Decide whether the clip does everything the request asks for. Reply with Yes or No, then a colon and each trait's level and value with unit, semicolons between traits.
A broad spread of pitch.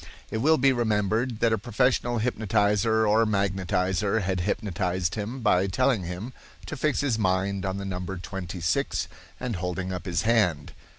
No: average, 3.5 semitones